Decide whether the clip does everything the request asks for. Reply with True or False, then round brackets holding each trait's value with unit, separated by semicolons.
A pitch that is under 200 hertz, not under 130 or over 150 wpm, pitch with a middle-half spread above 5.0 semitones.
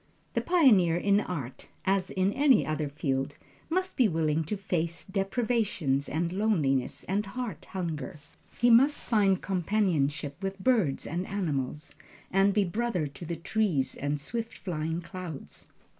True (185 Hz; 145 wpm; 5.4 semitones)